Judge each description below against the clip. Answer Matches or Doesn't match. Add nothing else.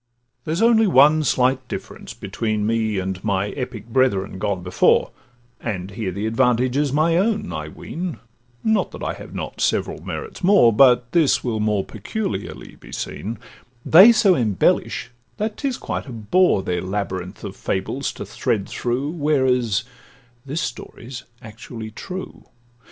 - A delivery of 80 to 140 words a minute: Doesn't match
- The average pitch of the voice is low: Matches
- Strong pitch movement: Matches